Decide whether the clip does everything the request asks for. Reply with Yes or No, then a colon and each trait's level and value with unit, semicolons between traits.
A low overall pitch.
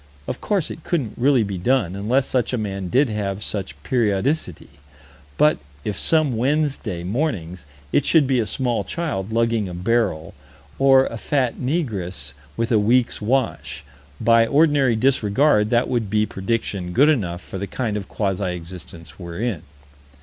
Yes: low, 115 Hz